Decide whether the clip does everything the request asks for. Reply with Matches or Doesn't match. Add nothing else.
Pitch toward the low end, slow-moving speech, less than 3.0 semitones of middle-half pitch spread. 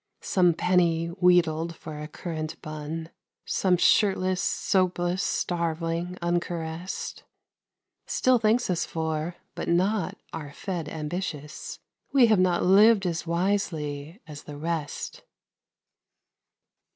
Doesn't match